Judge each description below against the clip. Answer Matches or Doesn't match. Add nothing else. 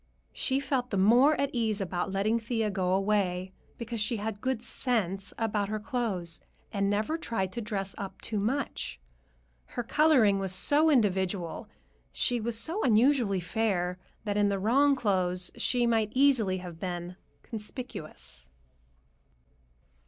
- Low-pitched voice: Doesn't match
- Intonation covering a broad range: Doesn't match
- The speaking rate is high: Doesn't match